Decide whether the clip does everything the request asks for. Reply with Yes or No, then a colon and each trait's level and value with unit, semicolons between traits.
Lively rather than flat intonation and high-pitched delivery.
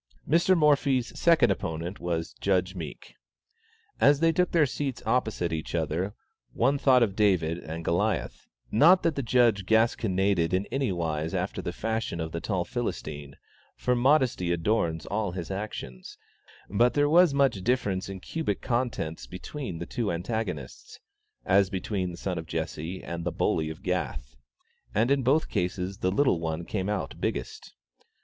No: wide, 6.7 semitones; low, 100 Hz